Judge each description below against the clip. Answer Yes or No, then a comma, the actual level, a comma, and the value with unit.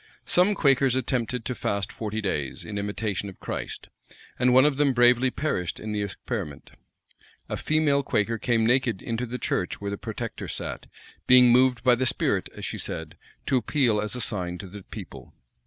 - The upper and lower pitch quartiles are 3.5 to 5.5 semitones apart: Yes, average, 4.0 semitones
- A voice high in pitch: No, low, 120 Hz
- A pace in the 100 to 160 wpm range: No, average, 185 wpm